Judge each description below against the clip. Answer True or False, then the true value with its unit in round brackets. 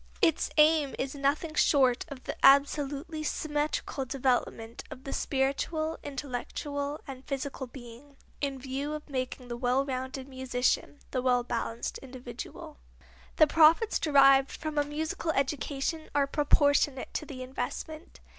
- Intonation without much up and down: True (2.3 semitones)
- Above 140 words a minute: False (135 wpm)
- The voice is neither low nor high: False (275 Hz)